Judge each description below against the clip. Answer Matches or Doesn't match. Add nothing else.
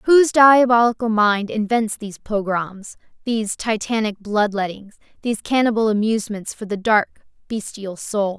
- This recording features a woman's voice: Matches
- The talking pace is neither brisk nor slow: Doesn't match